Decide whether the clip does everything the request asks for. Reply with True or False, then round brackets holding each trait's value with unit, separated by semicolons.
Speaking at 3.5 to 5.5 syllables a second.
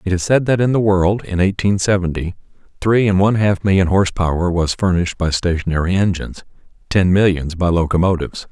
False (6.0 syllables/s)